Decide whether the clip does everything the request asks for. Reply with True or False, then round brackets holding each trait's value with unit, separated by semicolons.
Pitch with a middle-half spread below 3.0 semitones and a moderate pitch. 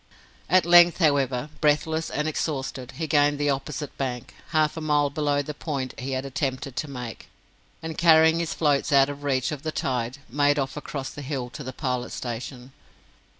True (2.6 semitones; 145 Hz)